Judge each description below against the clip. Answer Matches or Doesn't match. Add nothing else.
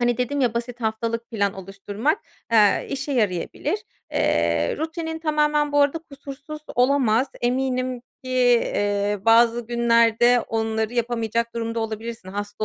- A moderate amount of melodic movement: Matches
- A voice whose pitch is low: Doesn't match